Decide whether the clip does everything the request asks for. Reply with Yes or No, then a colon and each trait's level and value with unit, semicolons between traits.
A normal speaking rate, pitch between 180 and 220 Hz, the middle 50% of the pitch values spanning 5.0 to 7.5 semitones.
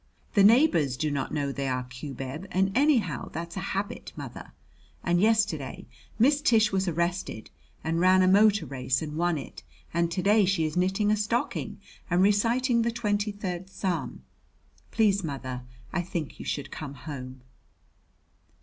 Yes: average, 160 wpm; medium, 185 Hz; wide, 5.6 semitones